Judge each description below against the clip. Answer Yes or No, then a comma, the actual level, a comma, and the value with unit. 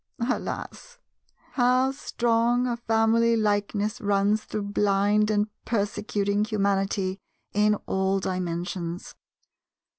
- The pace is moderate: No, slow, 90 wpm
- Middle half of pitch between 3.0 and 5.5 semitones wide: No, narrow, 2.5 semitones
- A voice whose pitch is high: Yes, high, 210 Hz